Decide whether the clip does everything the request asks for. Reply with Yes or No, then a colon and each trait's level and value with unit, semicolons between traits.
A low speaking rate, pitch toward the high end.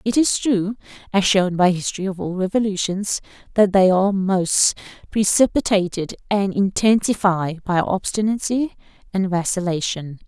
Yes: slow, 130 wpm; high, 195 Hz